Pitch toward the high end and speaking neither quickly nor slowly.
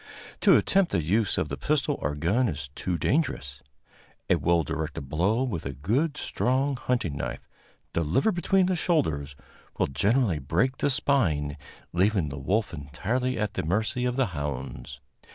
No: very low, 95 Hz; average, 160 wpm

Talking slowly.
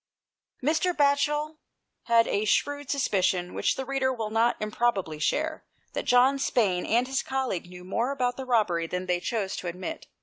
No: average, 170 wpm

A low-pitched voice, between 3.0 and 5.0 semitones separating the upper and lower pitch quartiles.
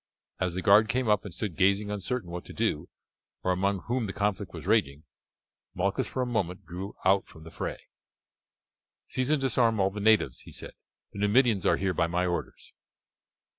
Yes: low, 100 Hz; average, 3.3 semitones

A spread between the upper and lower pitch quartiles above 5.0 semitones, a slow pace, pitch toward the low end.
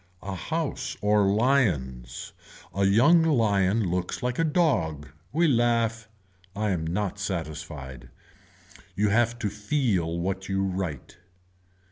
Yes: wide, 5.5 semitones; slow, 120 wpm; low, 100 Hz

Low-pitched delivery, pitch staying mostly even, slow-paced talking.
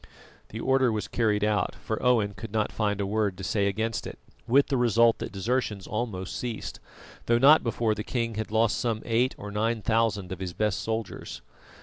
No: low, 110 Hz; narrow, 2.2 semitones; average, 200 wpm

